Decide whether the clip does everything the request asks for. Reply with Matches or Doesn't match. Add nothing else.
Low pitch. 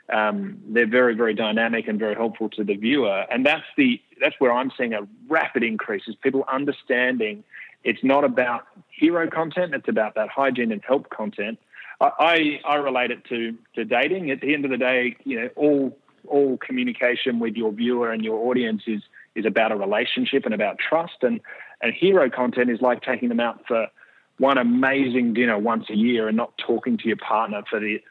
Matches